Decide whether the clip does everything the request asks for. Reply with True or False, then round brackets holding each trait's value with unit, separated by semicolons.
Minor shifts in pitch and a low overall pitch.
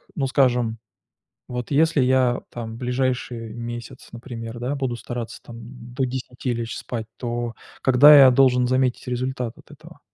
True (1.7 semitones; 125 Hz)